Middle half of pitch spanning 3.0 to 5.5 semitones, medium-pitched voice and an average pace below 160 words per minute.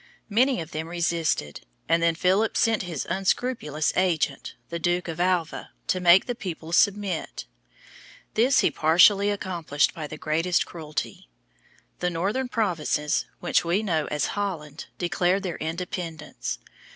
Yes: average, 3.4 semitones; medium, 175 Hz; average, 140 wpm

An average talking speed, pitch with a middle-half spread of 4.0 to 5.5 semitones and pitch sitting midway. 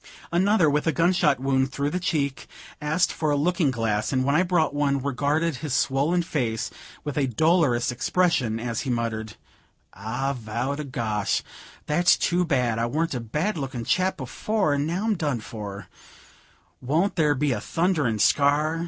Yes: average, 175 wpm; average, 5.1 semitones; medium, 145 Hz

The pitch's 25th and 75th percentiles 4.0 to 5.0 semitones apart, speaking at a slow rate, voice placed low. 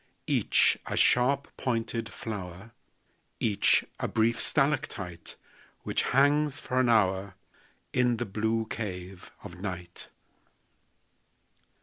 Yes: average, 4.7 semitones; slow, 100 wpm; low, 110 Hz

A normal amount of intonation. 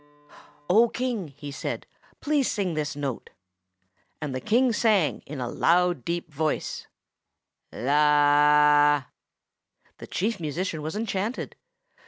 No: wide, 5.8 semitones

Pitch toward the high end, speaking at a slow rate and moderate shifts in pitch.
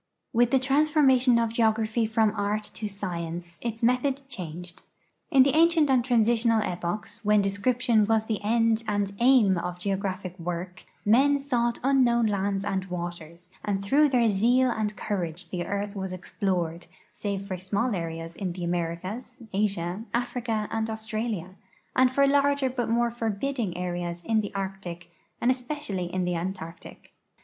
No: high, 210 Hz; average, 155 wpm; average, 4.6 semitones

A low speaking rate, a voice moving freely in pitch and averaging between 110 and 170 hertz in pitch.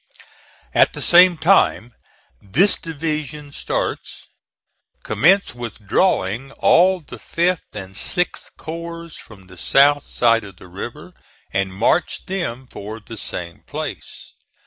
Yes: slow, 125 wpm; wide, 8.5 semitones; low, 135 Hz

